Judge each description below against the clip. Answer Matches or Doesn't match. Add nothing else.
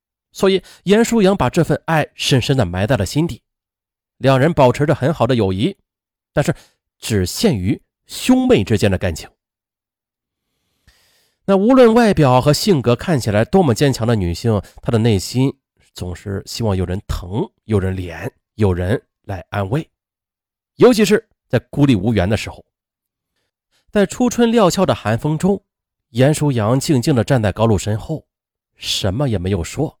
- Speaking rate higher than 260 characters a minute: Doesn't match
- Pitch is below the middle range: Matches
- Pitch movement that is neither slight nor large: Doesn't match